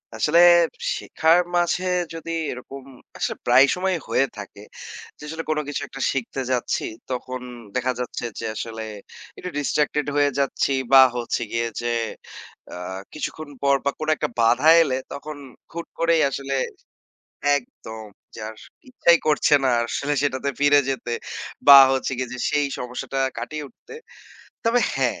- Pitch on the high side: No, medium, 140 Hz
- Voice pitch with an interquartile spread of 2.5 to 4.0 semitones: Yes, average, 3.5 semitones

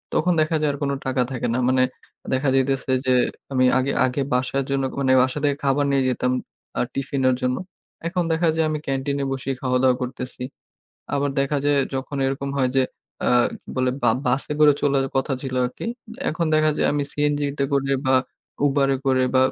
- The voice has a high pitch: No, low, 135 Hz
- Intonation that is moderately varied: No, narrow, 1.8 semitones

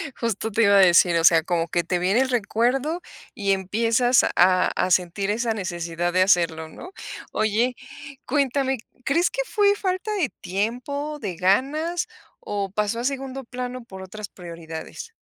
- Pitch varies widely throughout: Yes, wide, 6.4 semitones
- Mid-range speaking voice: No, high, 220 Hz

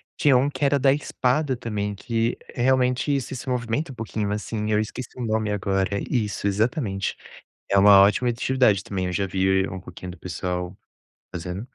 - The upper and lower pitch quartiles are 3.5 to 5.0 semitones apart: Yes, average, 4.5 semitones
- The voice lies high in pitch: No, low, 110 Hz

